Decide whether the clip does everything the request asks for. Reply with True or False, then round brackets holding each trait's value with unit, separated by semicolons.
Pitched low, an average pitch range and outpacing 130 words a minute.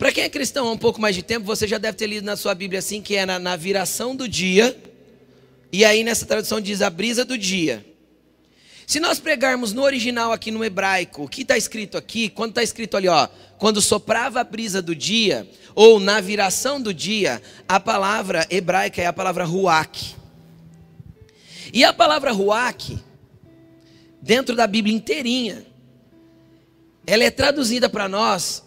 False (210 Hz; 4.2 semitones; 175 wpm)